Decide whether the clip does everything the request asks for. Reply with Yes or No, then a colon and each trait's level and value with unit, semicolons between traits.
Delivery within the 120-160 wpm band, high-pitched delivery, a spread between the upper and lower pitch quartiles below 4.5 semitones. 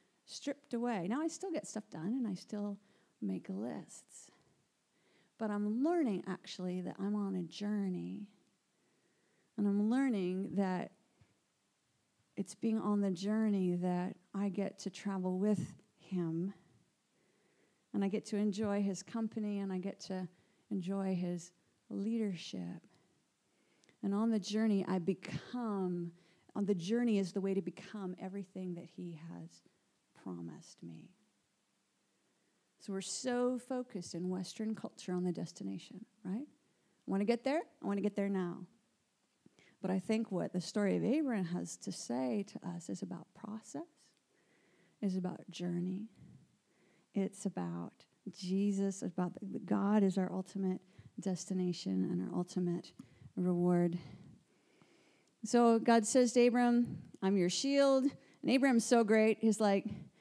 Yes: average, 140 wpm; high, 195 Hz; average, 3.3 semitones